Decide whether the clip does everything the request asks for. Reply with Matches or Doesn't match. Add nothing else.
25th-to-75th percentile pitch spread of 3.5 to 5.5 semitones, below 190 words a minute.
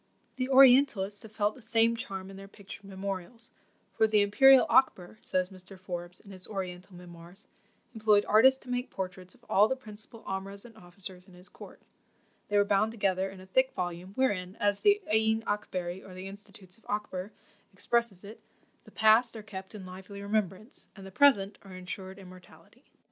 Doesn't match